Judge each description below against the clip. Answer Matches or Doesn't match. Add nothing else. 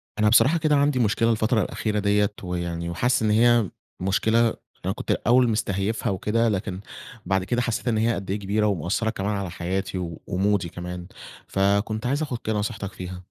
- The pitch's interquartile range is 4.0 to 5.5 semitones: Doesn't match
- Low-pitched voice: Matches